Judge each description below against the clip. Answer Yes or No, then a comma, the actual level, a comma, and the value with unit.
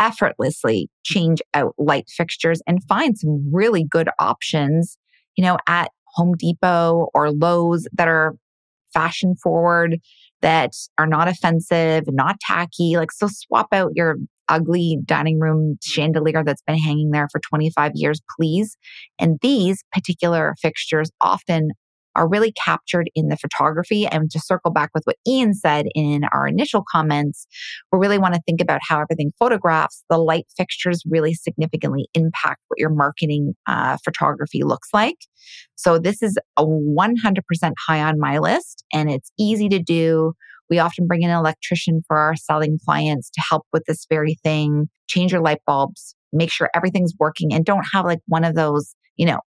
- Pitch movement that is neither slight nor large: No, narrow, 2.2 semitones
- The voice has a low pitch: No, medium, 165 Hz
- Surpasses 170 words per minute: No, average, 165 wpm